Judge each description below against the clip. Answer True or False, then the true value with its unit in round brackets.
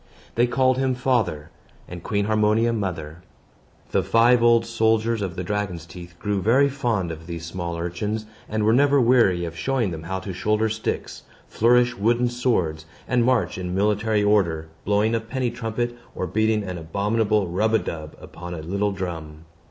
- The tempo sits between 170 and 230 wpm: True (175 wpm)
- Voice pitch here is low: True (105 Hz)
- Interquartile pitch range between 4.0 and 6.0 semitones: True (4.9 semitones)